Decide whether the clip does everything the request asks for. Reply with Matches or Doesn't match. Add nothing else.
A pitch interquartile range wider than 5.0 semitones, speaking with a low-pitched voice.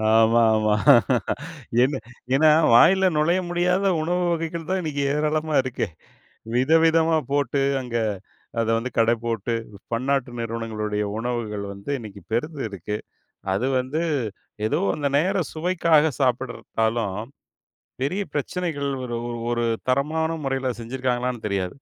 Matches